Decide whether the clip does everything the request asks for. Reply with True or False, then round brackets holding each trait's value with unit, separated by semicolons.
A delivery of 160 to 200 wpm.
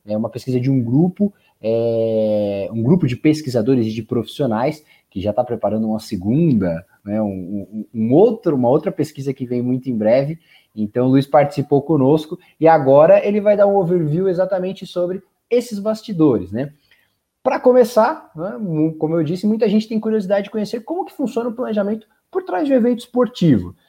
True (185 wpm)